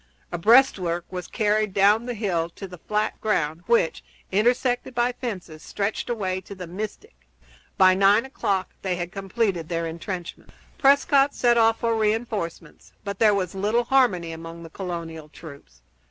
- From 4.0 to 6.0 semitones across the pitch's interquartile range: Yes, average, 4.9 semitones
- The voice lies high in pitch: Yes, high, 195 Hz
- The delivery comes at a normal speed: Yes, average, 160 wpm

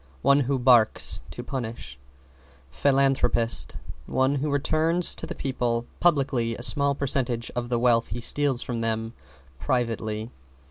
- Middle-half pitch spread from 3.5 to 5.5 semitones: No, average, 3.1 semitones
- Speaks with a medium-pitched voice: No, low, 125 Hz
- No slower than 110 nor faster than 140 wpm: Yes, slow, 135 wpm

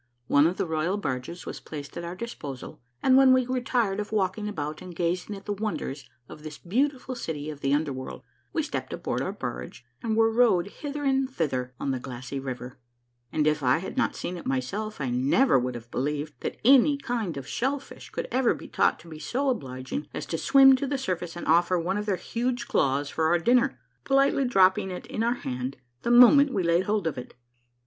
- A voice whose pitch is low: No, medium, 180 Hz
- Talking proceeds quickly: Yes, fast, 220 wpm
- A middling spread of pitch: No, wide, 8.8 semitones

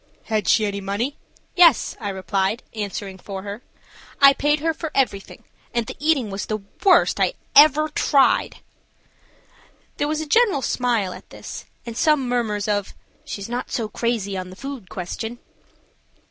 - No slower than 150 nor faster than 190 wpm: Yes, average, 160 wpm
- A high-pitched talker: Yes, high, 230 Hz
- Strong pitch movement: Yes, wide, 5.9 semitones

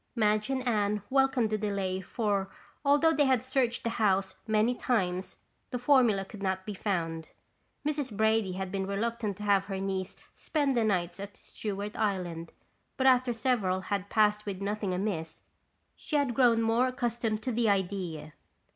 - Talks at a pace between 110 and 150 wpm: No, average, 165 wpm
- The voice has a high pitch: Yes, high, 210 Hz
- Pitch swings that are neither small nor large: Yes, average, 3.8 semitones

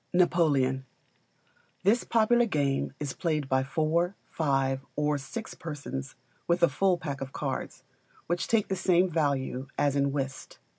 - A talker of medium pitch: Yes, medium, 150 Hz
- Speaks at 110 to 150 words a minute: Yes, average, 145 wpm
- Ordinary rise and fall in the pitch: Yes, average, 4.5 semitones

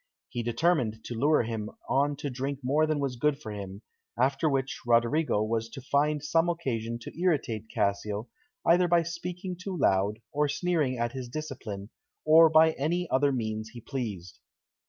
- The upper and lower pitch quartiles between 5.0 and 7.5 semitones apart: Yes, wide, 5.5 semitones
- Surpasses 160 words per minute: Yes, average, 170 wpm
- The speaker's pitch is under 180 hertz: Yes, low, 135 Hz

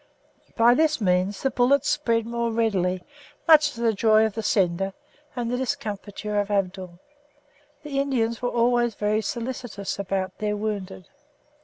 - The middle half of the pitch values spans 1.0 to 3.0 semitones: No, average, 3.5 semitones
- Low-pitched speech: No, high, 220 Hz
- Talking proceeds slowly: No, average, 150 wpm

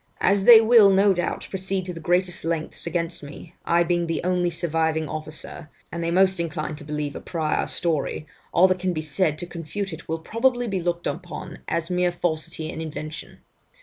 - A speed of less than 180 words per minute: No, average, 195 wpm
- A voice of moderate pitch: Yes, medium, 170 Hz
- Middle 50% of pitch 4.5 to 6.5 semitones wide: No, narrow, 2.6 semitones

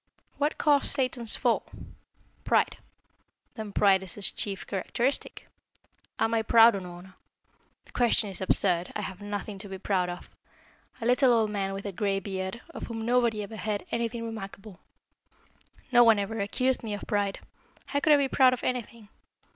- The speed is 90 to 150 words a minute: No, average, 170 wpm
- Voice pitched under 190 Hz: No, high, 215 Hz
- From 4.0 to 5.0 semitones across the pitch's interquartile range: No, average, 3.2 semitones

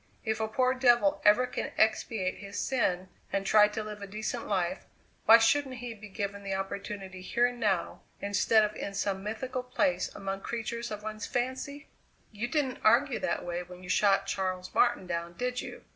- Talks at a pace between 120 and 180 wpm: No, average, 190 wpm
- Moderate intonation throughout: Yes, average, 3.8 semitones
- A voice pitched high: Yes, high, 210 Hz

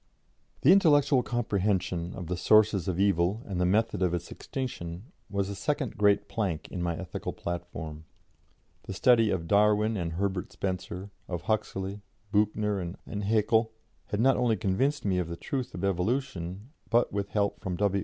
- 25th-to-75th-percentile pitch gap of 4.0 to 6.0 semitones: No, average, 3.6 semitones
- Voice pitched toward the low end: Yes, low, 100 Hz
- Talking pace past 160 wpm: Yes, average, 170 wpm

